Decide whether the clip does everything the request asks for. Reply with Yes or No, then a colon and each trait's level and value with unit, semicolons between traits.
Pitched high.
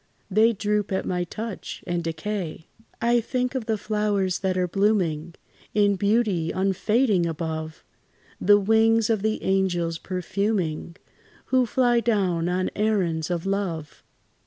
Yes: high, 195 Hz